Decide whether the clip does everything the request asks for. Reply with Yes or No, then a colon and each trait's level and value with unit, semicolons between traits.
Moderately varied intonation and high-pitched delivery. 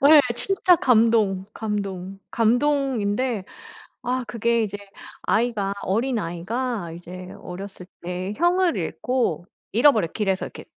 Yes: average, 4.9 semitones; high, 220 Hz